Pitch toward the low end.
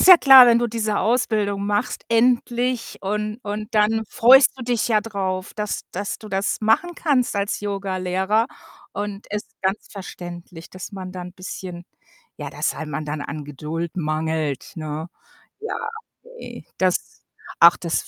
No: high, 200 Hz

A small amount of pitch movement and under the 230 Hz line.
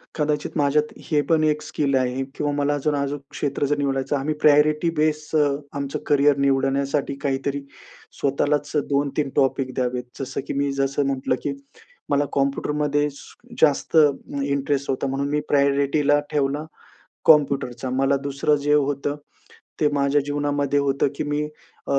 Yes: narrow, 1.2 semitones; medium, 140 Hz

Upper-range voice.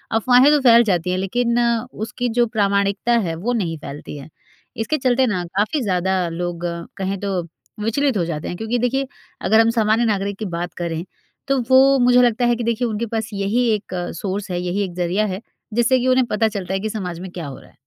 Yes: high, 210 Hz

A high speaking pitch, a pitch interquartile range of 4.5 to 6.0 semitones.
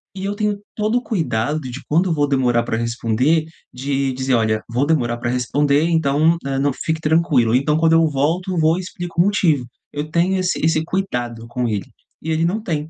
No: medium, 150 Hz; average, 5.0 semitones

